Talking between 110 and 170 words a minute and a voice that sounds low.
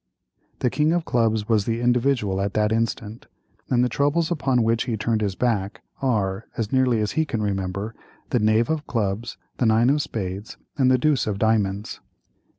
No: average, 185 wpm; low, 115 Hz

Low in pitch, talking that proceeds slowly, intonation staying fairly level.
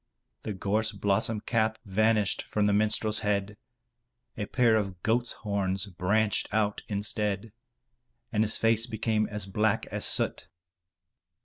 Yes: low, 105 Hz; slow, 130 wpm; narrow, 1.5 semitones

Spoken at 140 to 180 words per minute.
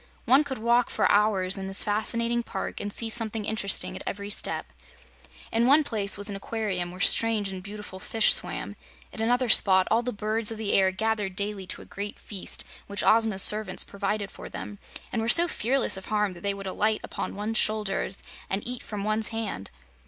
No: average, 200 wpm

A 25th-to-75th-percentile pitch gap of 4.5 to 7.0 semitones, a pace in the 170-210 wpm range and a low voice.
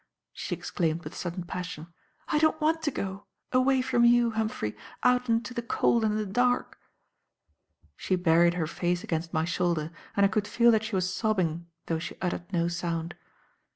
No: wide, 5.6 semitones; average, 180 wpm; high, 190 Hz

